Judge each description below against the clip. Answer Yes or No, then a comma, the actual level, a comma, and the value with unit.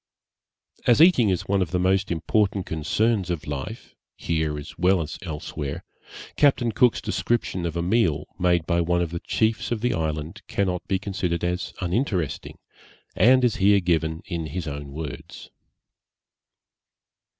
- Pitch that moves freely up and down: No, average, 4.1 semitones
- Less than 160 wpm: Yes, average, 150 wpm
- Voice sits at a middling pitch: No, very low, 90 Hz